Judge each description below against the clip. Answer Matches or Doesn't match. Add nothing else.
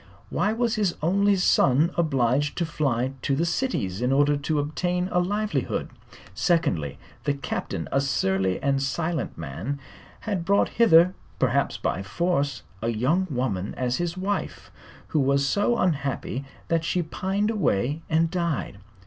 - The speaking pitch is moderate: Matches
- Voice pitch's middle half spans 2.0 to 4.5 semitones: Doesn't match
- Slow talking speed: Doesn't match